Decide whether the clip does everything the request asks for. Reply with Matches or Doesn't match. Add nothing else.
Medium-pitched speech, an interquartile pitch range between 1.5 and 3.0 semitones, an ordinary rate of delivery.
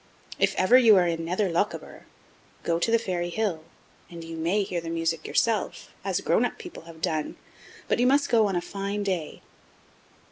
Doesn't match